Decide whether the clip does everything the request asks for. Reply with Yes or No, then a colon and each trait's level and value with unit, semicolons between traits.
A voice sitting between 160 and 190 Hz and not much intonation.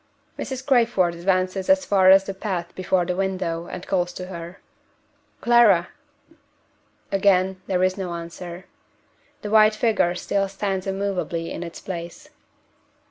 Yes: medium, 185 Hz; narrow, 2.1 semitones